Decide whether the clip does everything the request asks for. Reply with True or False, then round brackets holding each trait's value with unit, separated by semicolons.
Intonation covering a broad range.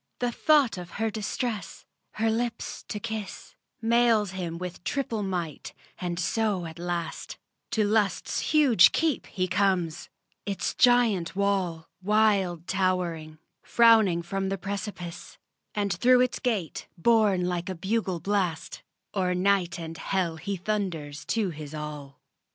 False (4.1 semitones)